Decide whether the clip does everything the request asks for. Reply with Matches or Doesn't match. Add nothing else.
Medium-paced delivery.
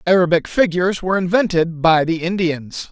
Matches